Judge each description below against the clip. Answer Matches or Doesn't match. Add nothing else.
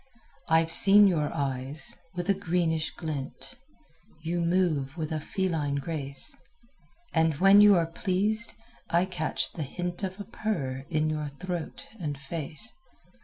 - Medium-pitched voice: Matches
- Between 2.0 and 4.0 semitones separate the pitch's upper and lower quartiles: Matches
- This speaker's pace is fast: Doesn't match